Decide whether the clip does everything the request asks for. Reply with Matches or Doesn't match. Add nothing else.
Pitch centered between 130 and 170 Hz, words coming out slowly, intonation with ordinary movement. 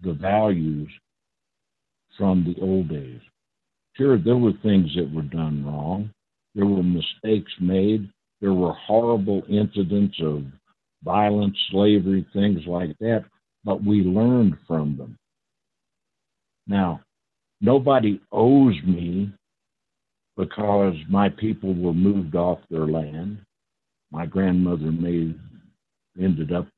Doesn't match